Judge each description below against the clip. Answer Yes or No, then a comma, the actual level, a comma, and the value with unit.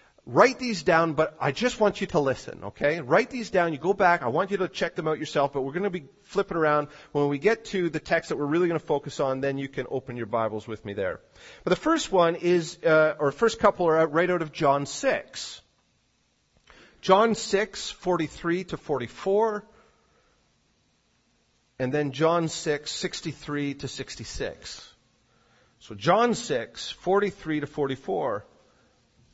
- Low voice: No, medium, 160 Hz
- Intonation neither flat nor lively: Yes, average, 4.9 semitones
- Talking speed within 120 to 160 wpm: No, average, 180 wpm